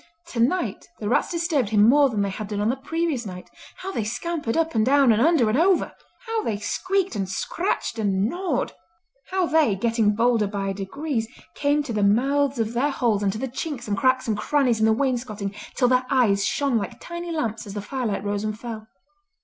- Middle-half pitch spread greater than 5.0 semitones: Yes, wide, 5.5 semitones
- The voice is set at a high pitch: Yes, high, 240 Hz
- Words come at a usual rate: No, fast, 210 wpm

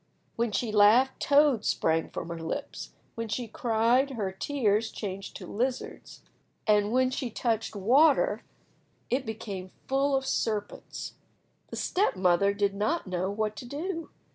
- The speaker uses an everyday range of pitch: Yes, average, 4.6 semitones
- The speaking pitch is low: No, high, 225 Hz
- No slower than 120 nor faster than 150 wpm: Yes, average, 145 wpm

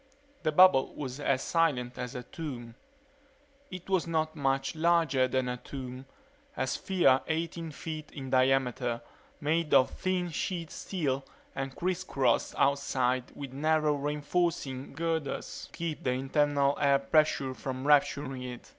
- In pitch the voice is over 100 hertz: Yes, medium, 140 Hz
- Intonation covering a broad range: No, average, 3.6 semitones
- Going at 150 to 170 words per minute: No, average, 140 wpm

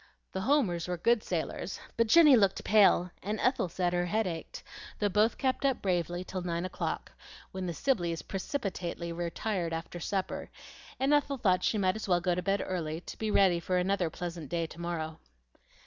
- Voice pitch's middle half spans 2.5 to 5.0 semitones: Yes, average, 3.6 semitones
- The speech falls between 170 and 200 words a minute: Yes, average, 190 wpm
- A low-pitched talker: No, medium, 185 Hz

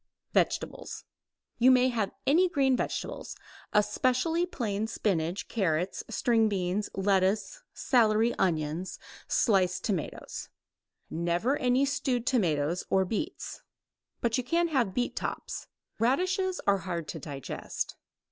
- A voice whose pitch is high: Yes, high, 220 Hz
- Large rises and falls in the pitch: Yes, wide, 5.7 semitones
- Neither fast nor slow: No, slow, 115 wpm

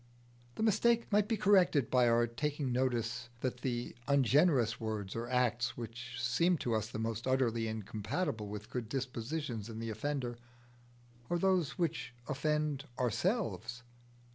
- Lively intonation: No, average, 4.7 semitones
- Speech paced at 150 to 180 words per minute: No, average, 140 wpm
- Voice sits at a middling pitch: No, low, 125 Hz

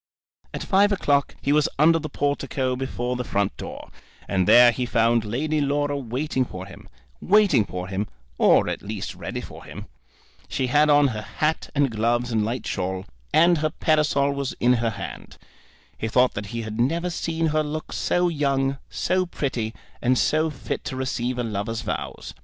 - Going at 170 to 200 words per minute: Yes, average, 180 wpm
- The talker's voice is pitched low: Yes, low, 130 Hz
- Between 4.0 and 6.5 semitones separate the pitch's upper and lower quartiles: Yes, average, 4.8 semitones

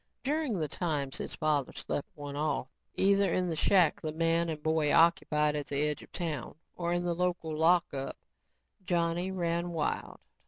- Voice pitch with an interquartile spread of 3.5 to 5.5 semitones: No, average, 2.7 semitones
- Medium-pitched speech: Yes, medium, 165 Hz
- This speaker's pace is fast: No, average, 170 wpm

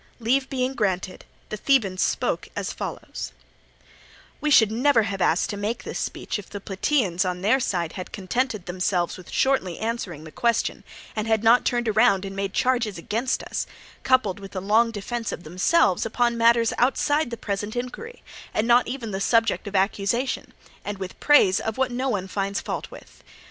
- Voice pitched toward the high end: Yes, high, 220 Hz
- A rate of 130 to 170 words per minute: No, average, 180 wpm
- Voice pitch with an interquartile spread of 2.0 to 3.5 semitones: No, average, 4.1 semitones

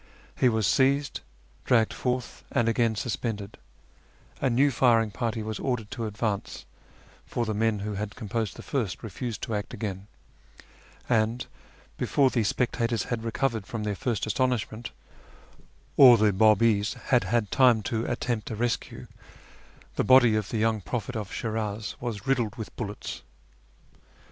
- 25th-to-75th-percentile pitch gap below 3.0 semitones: Yes, narrow, 2.4 semitones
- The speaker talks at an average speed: Yes, average, 150 wpm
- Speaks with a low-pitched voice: Yes, low, 115 Hz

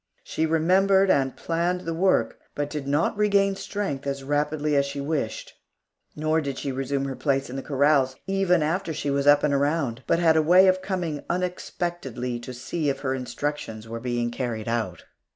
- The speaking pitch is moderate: Yes, medium, 145 Hz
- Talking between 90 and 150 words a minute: No, average, 190 wpm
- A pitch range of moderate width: Yes, average, 4.3 semitones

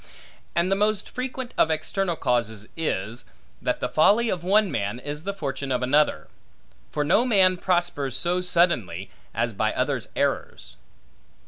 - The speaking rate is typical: Yes, average, 150 wpm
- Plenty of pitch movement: Yes, wide, 7.4 semitones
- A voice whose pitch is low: No, medium, 155 Hz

